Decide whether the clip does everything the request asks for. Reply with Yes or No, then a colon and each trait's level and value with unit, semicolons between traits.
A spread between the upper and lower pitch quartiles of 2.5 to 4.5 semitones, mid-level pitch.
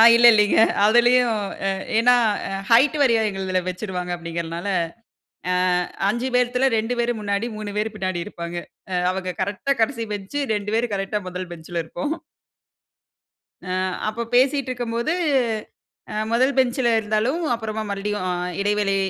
No: average, 3.9 semitones; high, 215 Hz